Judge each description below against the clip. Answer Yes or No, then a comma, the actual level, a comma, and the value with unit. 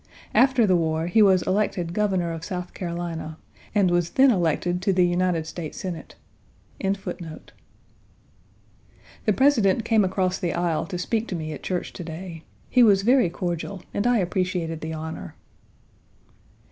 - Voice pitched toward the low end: No, medium, 180 Hz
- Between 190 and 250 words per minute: No, average, 160 wpm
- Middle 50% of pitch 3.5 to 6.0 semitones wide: No, average, 3.0 semitones